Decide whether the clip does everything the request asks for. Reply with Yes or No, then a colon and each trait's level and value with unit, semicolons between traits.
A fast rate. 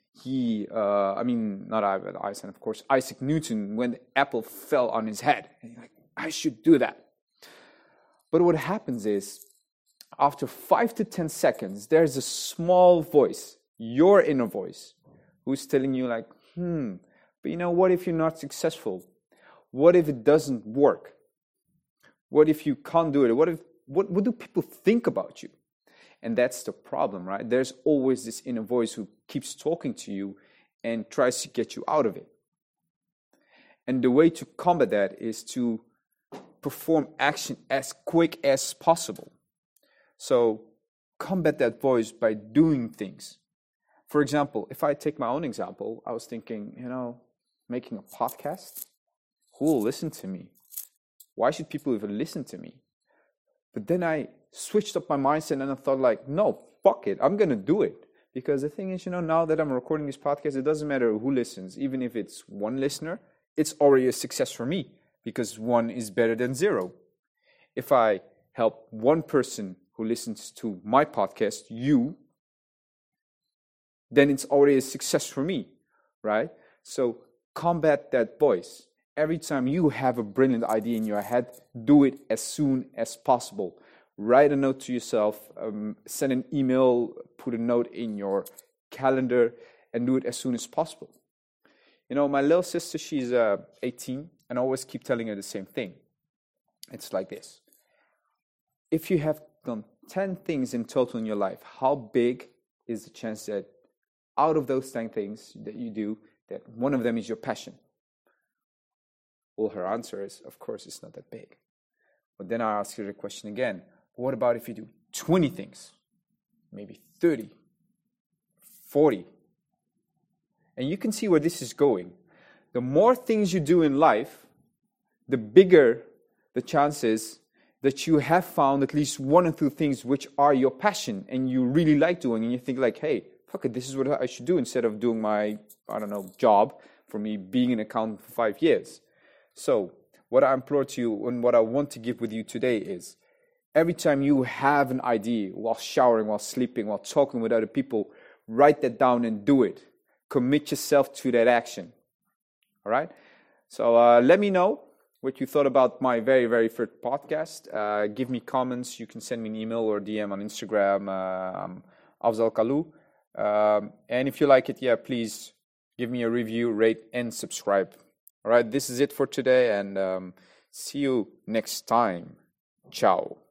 No: average, 180 wpm